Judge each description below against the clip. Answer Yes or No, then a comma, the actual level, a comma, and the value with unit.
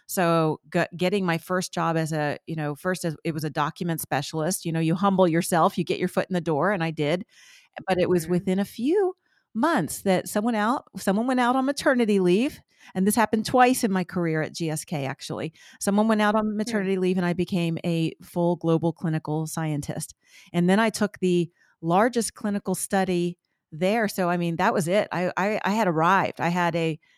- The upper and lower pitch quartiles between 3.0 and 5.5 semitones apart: Yes, average, 3.7 semitones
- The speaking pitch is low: No, medium, 180 Hz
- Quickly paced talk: Yes, fast, 210 wpm